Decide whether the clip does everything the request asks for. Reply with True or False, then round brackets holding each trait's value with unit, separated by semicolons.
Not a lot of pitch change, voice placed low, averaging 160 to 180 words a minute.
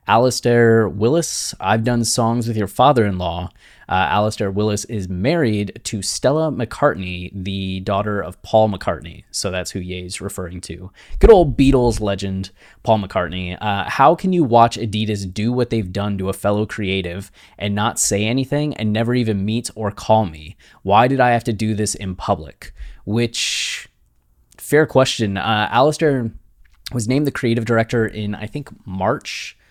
False (3.7 semitones; 105 Hz; 170 wpm)